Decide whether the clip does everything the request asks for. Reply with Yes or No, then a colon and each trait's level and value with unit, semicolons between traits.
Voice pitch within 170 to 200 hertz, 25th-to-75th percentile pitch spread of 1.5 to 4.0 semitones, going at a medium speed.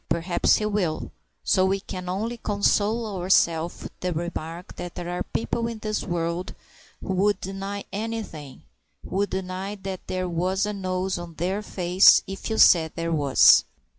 Yes: medium, 185 Hz; average, 2.7 semitones; average, 165 wpm